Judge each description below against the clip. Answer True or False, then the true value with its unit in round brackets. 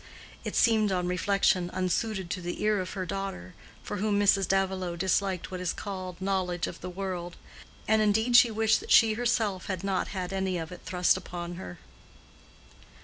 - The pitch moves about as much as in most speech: False (2.2 semitones)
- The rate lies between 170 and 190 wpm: True (180 wpm)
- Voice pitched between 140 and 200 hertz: True (190 Hz)